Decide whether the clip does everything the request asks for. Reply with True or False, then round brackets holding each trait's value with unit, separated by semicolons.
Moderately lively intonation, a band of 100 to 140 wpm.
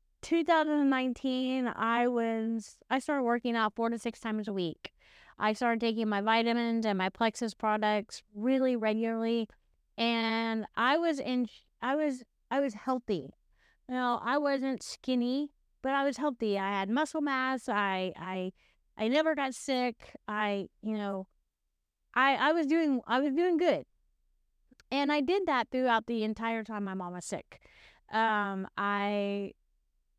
False (3.9 semitones; 155 wpm)